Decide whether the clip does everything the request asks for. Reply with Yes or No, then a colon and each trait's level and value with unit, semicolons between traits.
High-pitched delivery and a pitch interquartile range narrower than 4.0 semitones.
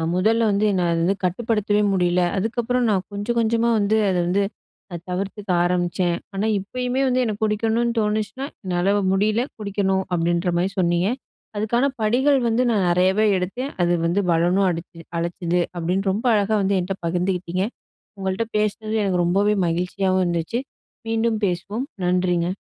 Yes: high, 195 Hz; average, 3.4 semitones